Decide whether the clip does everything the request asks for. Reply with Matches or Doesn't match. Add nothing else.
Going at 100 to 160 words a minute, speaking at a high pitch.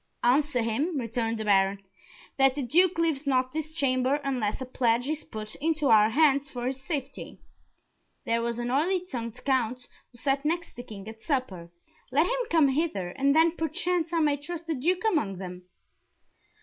Doesn't match